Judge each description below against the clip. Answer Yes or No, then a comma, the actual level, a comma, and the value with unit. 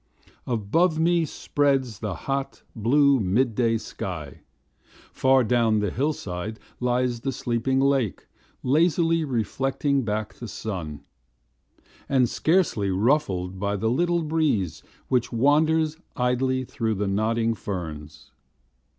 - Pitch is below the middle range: Yes, low, 125 Hz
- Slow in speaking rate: Yes, slow, 115 wpm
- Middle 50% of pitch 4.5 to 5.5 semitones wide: Yes, average, 5.1 semitones